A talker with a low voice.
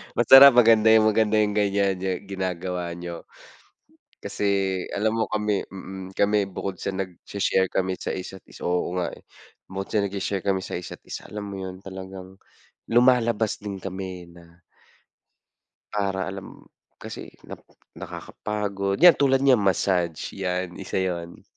Yes: very low, 95 Hz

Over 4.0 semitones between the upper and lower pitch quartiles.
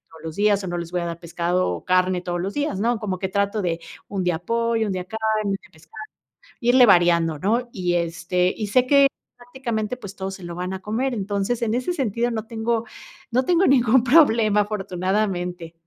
Yes: average, 4.5 semitones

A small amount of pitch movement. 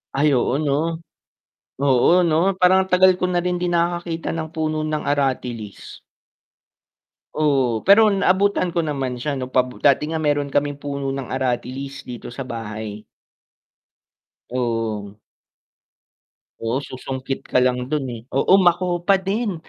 No: wide, 5.4 semitones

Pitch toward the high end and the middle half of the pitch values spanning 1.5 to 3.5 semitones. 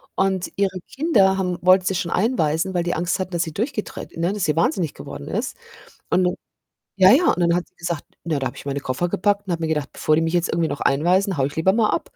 No: medium, 175 Hz; average, 2.9 semitones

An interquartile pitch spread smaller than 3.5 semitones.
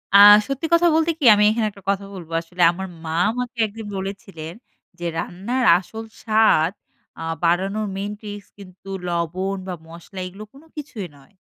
No: average, 3.8 semitones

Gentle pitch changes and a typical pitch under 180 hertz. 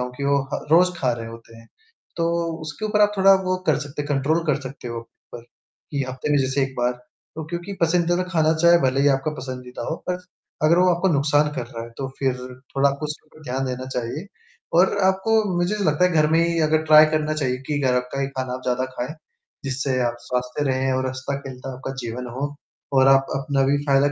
No: average, 3.9 semitones; medium, 140 Hz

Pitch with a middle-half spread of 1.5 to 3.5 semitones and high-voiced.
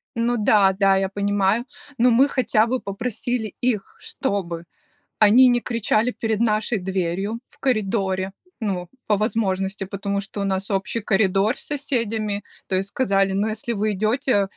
Yes: average, 3.0 semitones; high, 210 Hz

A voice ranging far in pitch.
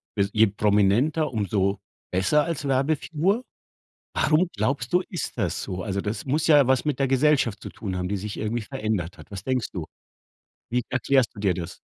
Yes: wide, 6.0 semitones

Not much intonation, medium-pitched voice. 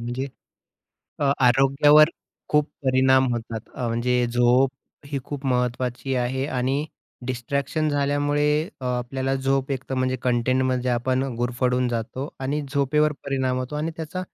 No: narrow, 2.1 semitones; low, 130 Hz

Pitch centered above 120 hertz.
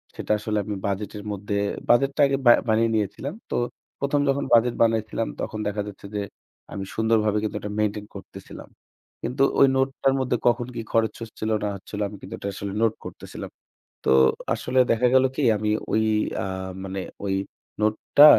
No: low, 110 Hz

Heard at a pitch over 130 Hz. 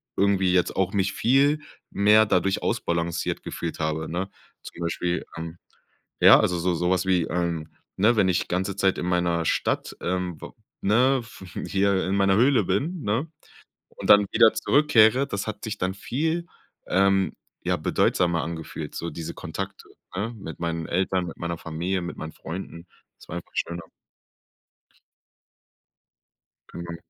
No: very low, 95 Hz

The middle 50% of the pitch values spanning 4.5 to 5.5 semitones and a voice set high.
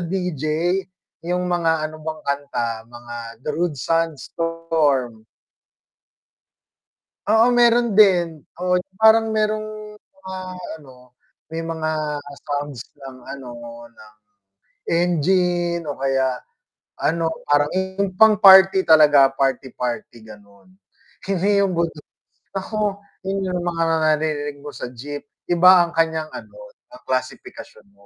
No: average, 5.0 semitones; medium, 165 Hz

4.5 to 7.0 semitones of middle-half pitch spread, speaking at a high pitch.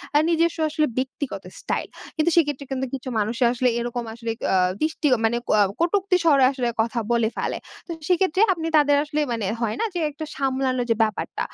Yes: average, 5.0 semitones; very high, 270 Hz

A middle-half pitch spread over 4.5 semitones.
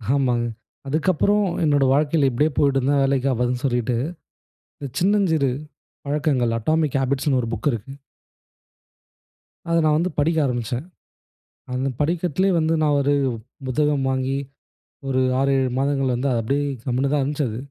No: average, 3.1 semitones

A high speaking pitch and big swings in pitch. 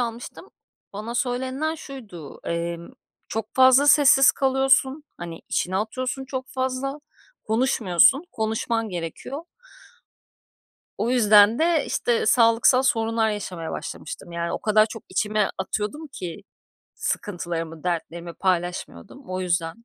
Yes: high, 220 Hz; wide, 6.5 semitones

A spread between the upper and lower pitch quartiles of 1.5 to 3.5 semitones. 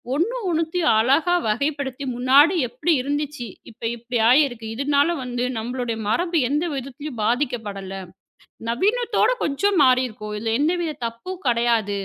No: average, 5.0 semitones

